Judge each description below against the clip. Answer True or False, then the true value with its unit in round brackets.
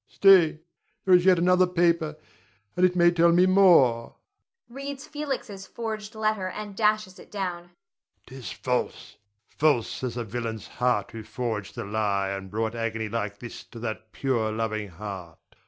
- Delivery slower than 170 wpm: True (155 wpm)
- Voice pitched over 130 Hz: True (140 Hz)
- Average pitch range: False (9.0 semitones)